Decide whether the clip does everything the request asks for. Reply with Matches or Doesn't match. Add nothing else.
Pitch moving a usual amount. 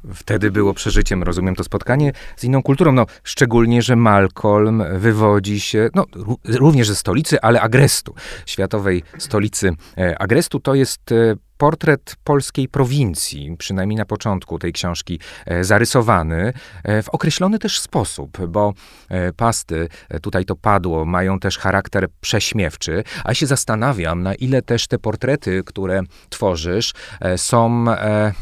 Matches